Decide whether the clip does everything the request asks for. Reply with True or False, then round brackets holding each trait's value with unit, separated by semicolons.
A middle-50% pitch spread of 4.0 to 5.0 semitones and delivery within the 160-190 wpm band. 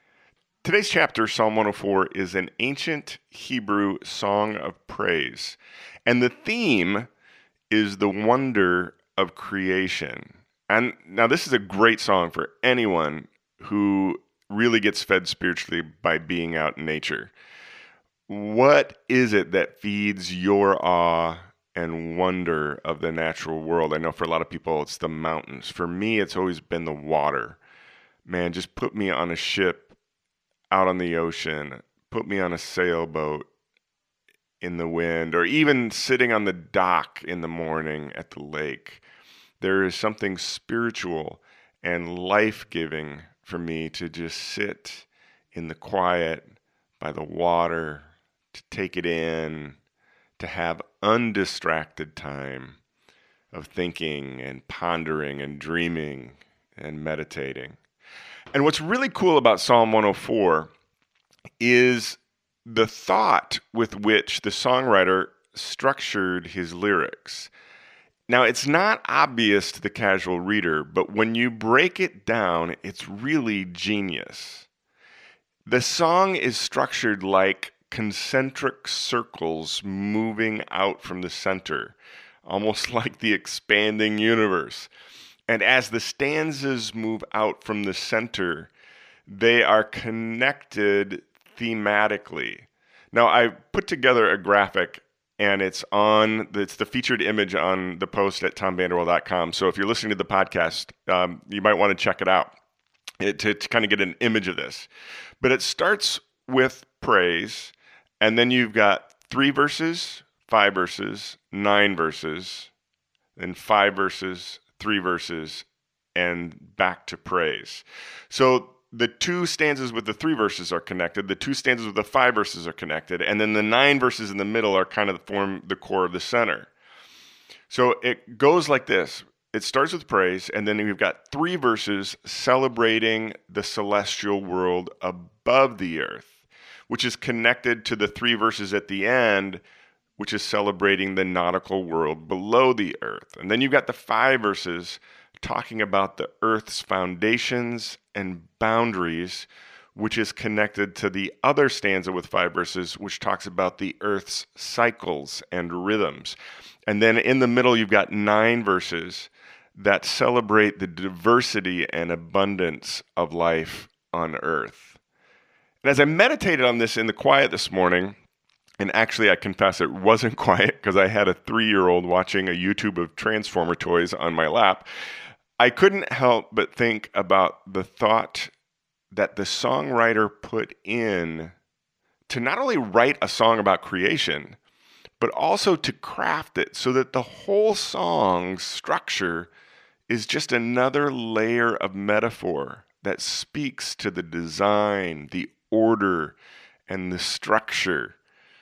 False (4.5 semitones; 145 wpm)